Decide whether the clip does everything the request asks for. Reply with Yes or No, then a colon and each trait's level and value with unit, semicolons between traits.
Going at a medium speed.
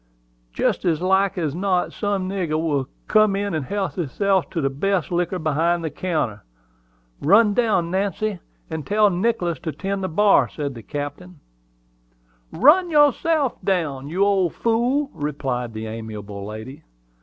Yes: average, 155 wpm